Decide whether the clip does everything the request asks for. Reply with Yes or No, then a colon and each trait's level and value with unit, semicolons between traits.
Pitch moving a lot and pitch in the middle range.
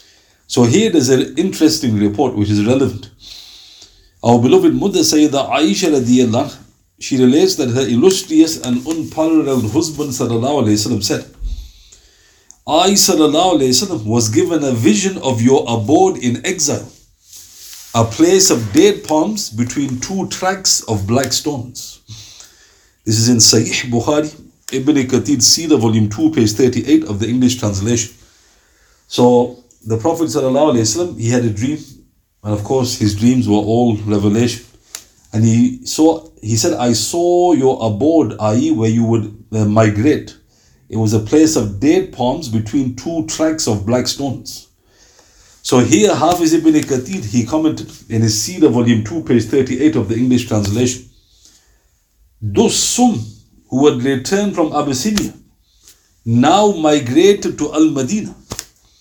No: wide, 5.7 semitones; low, 120 Hz